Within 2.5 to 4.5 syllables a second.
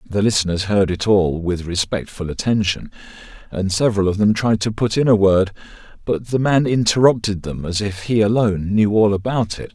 No: 5.3 syllables/s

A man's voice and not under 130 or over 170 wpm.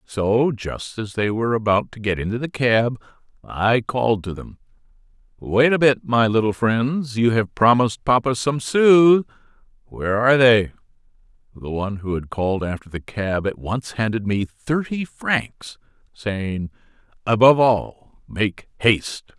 Yes: male; average, 150 wpm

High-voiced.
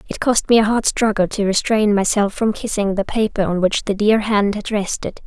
Yes: high, 210 Hz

